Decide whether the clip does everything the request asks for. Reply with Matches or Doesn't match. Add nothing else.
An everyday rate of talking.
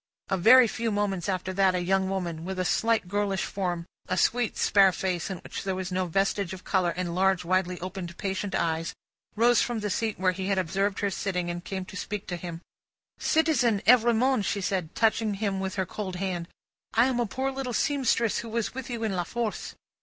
Doesn't match